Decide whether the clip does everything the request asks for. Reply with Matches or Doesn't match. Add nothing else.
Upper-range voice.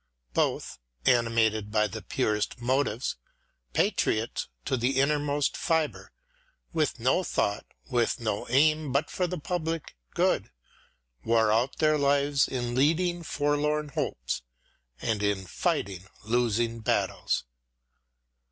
Doesn't match